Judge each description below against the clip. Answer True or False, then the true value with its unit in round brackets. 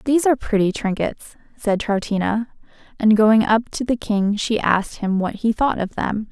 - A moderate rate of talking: True (190 wpm)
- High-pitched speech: True (215 Hz)